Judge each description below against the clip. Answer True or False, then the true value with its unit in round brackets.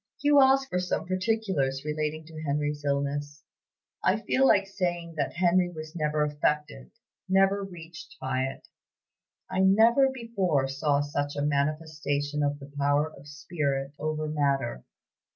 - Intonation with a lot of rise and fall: False (4.1 semitones)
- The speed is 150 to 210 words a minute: False (140 wpm)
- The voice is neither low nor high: True (150 Hz)